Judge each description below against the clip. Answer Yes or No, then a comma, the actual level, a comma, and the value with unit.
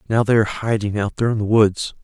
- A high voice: No, low, 110 Hz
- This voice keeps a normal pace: No, fast, 265 wpm